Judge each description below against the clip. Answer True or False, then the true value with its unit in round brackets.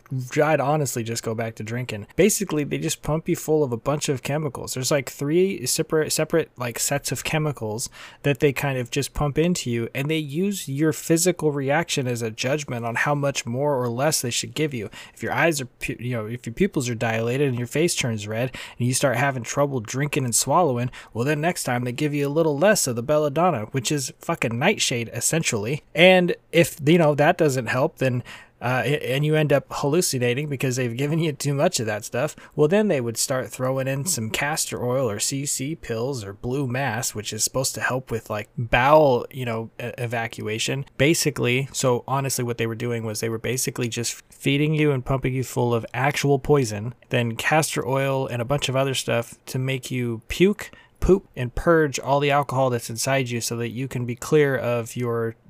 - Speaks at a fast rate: True (215 wpm)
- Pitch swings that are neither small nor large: True (3.9 semitones)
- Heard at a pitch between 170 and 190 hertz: False (135 Hz)